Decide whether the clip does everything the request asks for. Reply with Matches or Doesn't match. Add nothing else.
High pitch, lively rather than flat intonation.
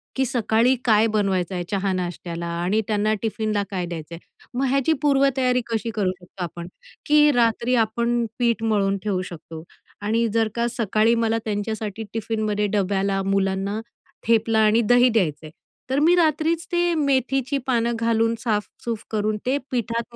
Doesn't match